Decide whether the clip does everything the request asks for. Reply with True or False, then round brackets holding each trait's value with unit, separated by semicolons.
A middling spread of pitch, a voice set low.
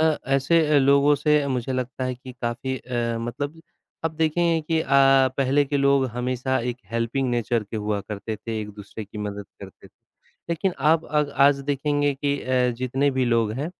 True (3.5 semitones; 130 Hz)